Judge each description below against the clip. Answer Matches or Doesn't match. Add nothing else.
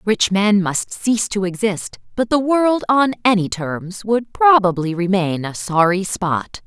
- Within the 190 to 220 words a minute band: Doesn't match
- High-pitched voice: Matches